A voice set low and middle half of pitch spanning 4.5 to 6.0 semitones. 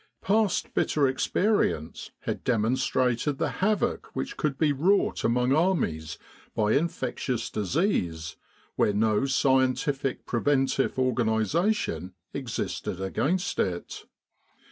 Yes: low, 130 Hz; wide, 5.6 semitones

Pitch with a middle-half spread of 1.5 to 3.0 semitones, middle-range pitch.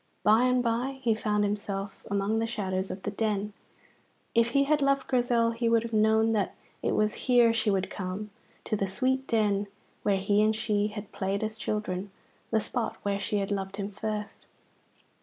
No: narrow, 2.4 semitones; high, 215 Hz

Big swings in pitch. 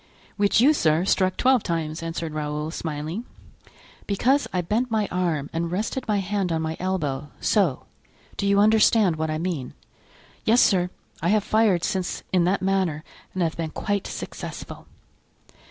No: average, 4.2 semitones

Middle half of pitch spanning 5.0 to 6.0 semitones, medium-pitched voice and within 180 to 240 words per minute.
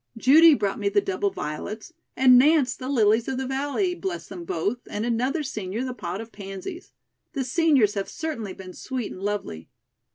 No: average, 5.3 semitones; high, 235 Hz; average, 185 wpm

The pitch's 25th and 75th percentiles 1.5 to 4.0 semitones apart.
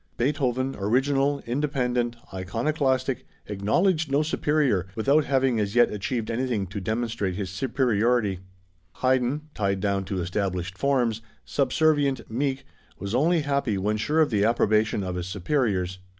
No: wide, 5.5 semitones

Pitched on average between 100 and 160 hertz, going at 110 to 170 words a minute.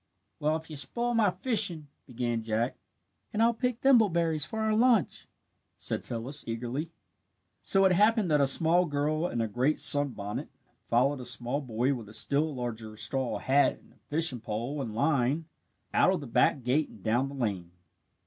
No: medium, 140 Hz; average, 180 wpm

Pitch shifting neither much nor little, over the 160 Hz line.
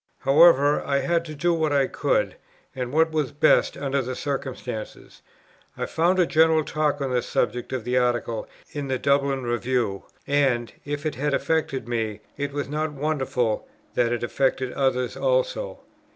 No: average, 3.6 semitones; medium, 140 Hz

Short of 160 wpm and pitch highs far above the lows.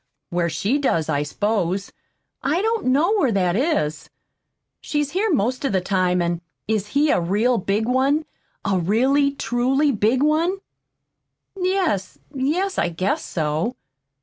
Yes: average, 150 wpm; wide, 7.9 semitones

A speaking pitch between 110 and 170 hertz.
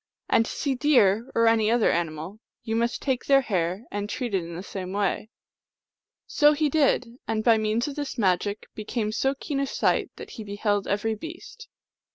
No: high, 220 Hz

